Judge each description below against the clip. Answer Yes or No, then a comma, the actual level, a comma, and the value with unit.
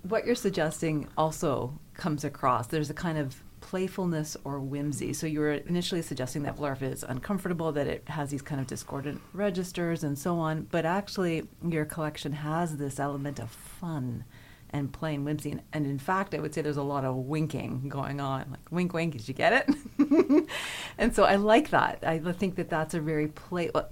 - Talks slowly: No, average, 195 wpm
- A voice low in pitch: No, medium, 155 Hz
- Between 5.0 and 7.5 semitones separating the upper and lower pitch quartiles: No, average, 3.7 semitones